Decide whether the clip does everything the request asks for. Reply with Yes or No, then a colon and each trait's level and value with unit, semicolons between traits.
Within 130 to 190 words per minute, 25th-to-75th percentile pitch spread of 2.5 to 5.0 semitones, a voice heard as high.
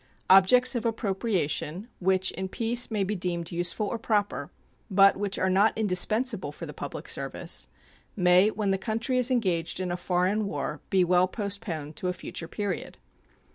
Yes: average, 170 wpm; average, 3.2 semitones; high, 195 Hz